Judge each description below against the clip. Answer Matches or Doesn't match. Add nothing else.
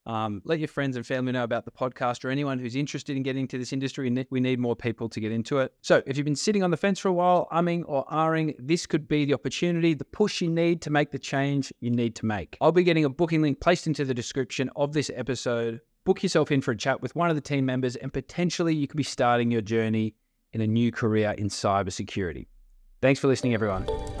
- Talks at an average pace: Doesn't match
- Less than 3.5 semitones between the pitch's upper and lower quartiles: Doesn't match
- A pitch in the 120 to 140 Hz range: Matches